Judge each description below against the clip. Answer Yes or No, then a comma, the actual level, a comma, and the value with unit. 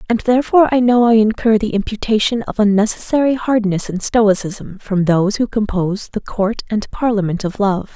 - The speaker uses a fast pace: No, average, 175 wpm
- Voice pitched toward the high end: Yes, high, 215 Hz